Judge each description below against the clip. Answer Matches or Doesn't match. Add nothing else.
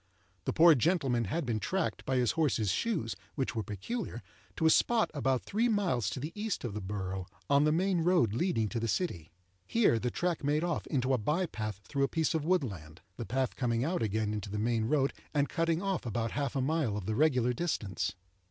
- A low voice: Matches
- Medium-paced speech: Doesn't match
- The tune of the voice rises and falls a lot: Matches